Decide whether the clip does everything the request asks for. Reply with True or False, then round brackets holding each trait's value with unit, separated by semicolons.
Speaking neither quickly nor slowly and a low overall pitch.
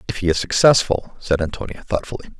True (175 wpm; 95 Hz)